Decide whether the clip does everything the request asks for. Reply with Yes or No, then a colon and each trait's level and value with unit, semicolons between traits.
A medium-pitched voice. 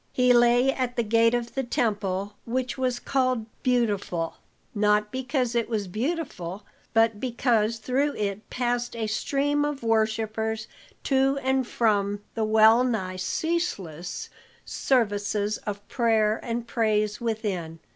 No: high, 230 Hz